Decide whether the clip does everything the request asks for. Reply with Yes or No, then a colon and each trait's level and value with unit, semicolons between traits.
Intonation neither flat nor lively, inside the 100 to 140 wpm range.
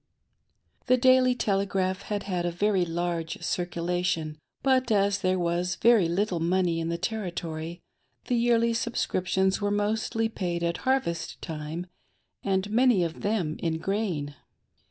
Yes: average, 4.0 semitones; slow, 135 wpm